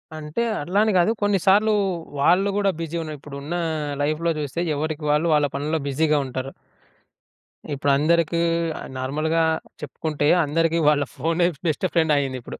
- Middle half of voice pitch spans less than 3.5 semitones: Yes, average, 2.8 semitones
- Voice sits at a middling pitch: Yes, medium, 155 Hz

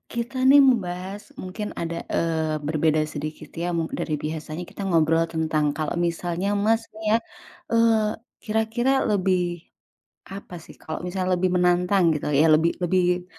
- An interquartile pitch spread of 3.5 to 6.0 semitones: Yes, average, 3.9 semitones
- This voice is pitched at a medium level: Yes, medium, 180 Hz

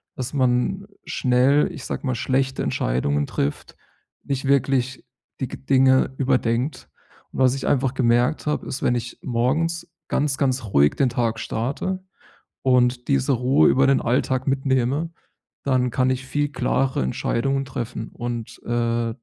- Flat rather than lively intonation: Yes, narrow, 2.2 semitones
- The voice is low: Yes, low, 130 Hz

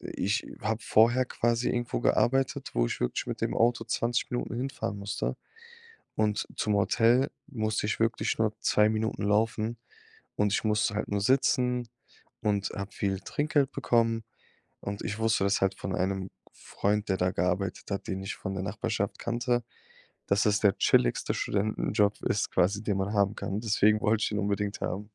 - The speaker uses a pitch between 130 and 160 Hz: No, low, 105 Hz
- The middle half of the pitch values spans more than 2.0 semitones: Yes, average, 2.7 semitones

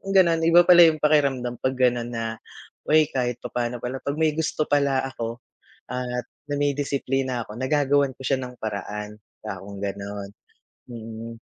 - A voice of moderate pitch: No, low, 125 Hz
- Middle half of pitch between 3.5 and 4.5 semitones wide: Yes, average, 3.8 semitones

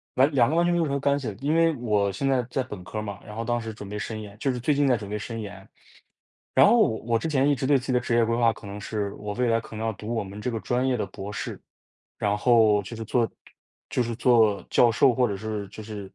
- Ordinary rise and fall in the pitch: Yes, average, 3.4 semitones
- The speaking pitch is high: No, low, 115 Hz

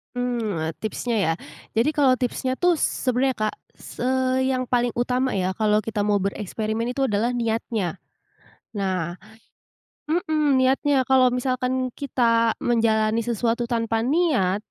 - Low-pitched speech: No, high, 240 Hz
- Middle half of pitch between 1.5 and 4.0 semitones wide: Yes, average, 3.1 semitones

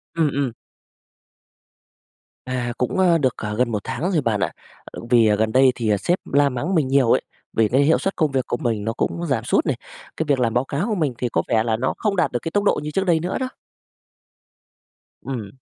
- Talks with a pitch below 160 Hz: Yes, low, 135 Hz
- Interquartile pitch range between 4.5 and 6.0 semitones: Yes, wide, 5.5 semitones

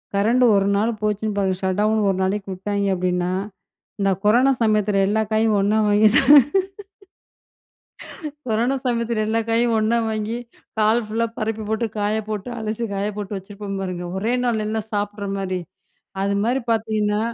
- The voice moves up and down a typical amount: No, narrow, 1.8 semitones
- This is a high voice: Yes, high, 210 Hz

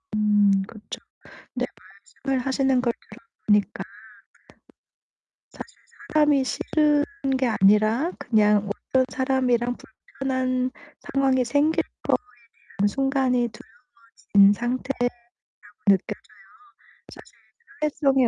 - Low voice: No, very high, 255 Hz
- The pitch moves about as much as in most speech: Yes, average, 4.0 semitones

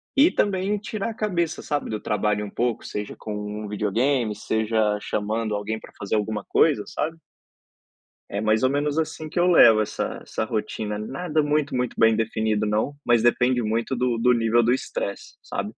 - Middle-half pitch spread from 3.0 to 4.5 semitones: No, average, 5.3 semitones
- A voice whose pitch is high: No, low, 115 Hz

